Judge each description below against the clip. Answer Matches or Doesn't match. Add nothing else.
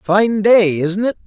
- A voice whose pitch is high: Matches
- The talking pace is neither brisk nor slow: Matches